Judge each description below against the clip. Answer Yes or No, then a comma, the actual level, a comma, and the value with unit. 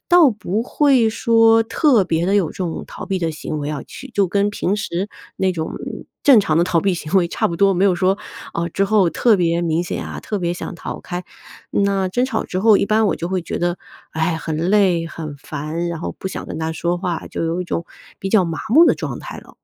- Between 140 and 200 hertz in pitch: Yes, medium, 185 Hz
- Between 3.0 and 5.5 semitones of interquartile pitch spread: Yes, average, 3.5 semitones